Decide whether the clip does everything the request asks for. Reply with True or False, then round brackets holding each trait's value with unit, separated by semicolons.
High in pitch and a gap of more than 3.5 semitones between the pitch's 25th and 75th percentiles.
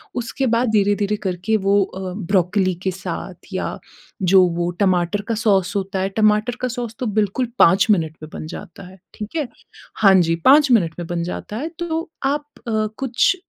True (200 Hz; 4.0 semitones)